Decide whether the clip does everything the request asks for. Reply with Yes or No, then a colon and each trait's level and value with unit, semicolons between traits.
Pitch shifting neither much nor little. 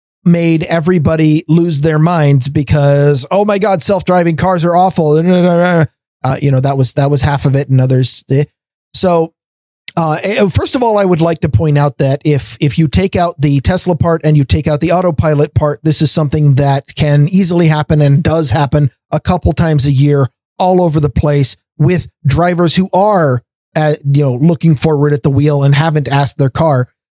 Yes: average, 3.2 semitones